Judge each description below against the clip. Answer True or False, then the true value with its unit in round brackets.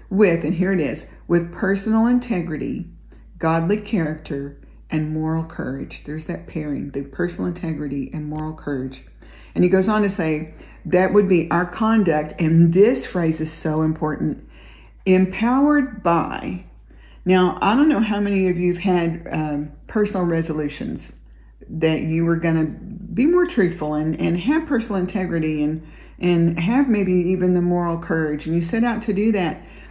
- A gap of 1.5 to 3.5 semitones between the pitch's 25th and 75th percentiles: False (4.0 semitones)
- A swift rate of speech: False (165 wpm)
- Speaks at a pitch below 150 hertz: False (170 Hz)